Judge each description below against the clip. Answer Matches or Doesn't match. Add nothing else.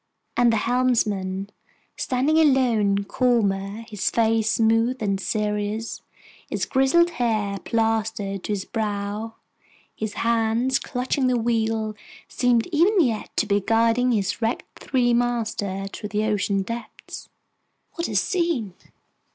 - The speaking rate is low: Matches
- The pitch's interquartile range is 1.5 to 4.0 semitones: Matches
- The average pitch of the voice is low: Doesn't match